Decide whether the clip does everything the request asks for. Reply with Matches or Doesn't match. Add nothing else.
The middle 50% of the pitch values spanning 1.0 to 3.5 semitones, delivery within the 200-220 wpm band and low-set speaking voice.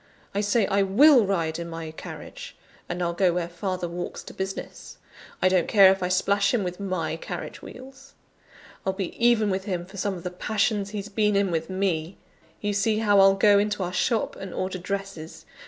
Doesn't match